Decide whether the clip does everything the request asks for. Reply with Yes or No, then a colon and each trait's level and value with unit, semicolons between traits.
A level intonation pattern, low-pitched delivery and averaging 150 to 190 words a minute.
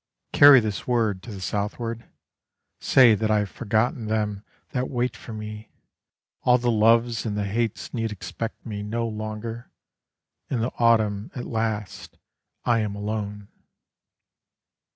No: narrow, 1.9 semitones; low, 110 Hz; average, 140 wpm